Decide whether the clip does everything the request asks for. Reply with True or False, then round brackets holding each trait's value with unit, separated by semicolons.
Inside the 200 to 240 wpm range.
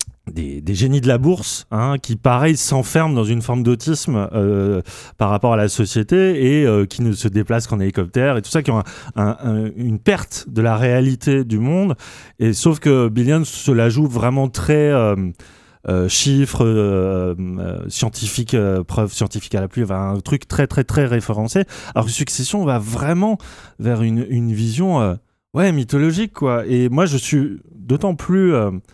False (185 wpm)